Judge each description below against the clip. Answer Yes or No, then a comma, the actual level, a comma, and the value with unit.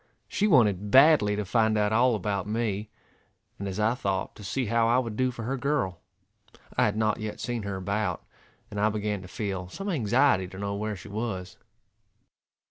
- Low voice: Yes, low, 105 Hz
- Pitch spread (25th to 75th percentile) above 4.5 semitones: No, average, 2.9 semitones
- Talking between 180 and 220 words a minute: Yes, average, 195 wpm